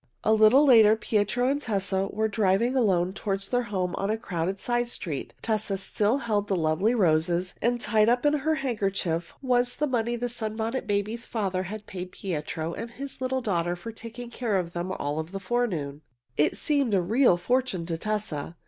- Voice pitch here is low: No, high, 210 Hz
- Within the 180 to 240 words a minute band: Yes, average, 185 wpm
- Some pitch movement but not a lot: Yes, average, 4.7 semitones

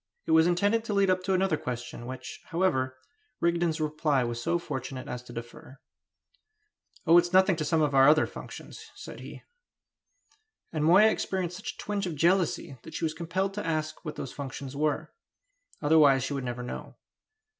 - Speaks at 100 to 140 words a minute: No, average, 180 wpm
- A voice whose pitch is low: No, medium, 155 Hz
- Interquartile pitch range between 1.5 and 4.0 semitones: No, average, 5.1 semitones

